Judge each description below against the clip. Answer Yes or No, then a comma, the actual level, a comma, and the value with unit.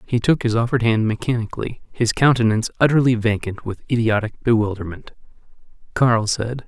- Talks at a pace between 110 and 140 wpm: Yes, slow, 135 wpm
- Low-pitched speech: Yes, low, 115 Hz